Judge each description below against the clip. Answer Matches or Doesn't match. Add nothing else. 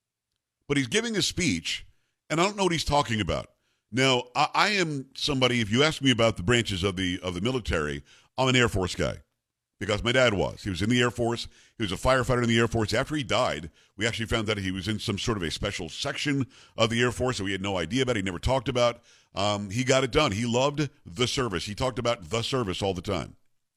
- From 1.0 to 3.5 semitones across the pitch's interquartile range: Doesn't match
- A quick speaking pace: Matches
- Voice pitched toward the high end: Doesn't match